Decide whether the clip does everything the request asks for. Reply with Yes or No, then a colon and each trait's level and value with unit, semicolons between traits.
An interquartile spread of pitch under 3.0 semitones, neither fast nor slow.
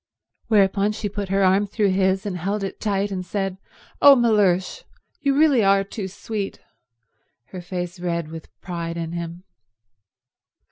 Yes: narrow, 2.6 semitones; average, 145 wpm